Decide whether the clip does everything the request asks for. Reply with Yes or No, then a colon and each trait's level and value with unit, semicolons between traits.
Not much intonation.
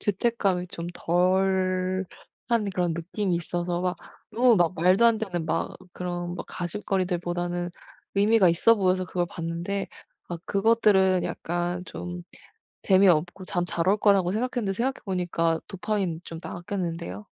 Yes: narrow, 2.1 semitones